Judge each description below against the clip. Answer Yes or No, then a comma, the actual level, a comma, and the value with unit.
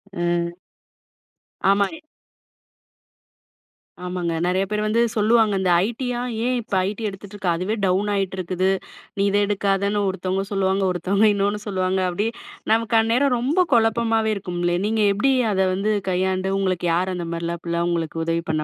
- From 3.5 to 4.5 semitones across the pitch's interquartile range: No, average, 2.9 semitones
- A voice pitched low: No, high, 195 Hz